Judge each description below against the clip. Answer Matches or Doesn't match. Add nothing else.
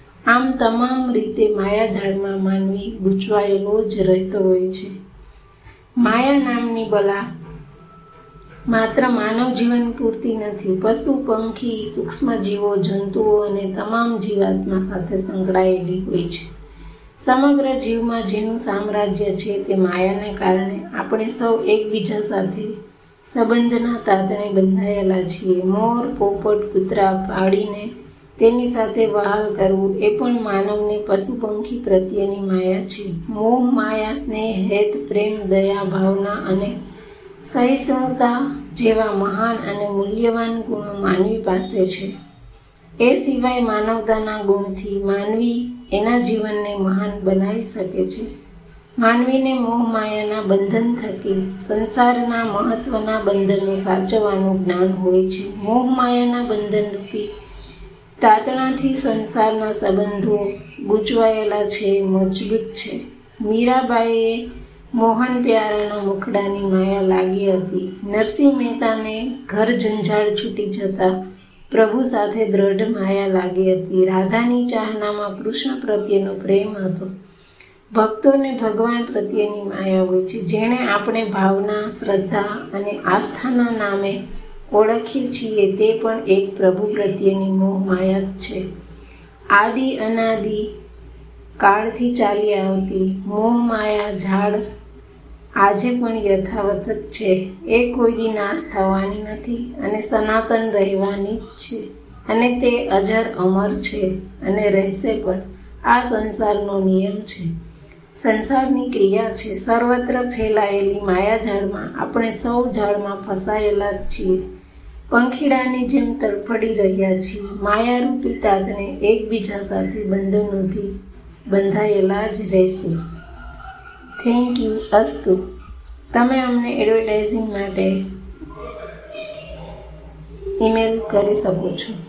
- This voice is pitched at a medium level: Doesn't match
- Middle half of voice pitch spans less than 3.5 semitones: Matches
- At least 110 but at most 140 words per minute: Doesn't match